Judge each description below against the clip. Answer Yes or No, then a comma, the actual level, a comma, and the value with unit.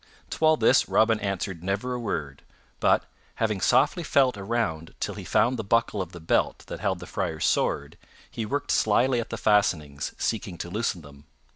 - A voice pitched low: Yes, low, 105 Hz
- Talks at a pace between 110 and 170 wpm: No, average, 185 wpm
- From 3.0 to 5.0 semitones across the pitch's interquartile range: No, wide, 5.4 semitones